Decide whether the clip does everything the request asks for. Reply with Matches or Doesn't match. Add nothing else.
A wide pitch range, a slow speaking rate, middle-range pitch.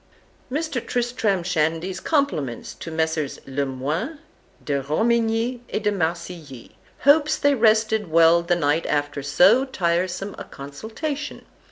Matches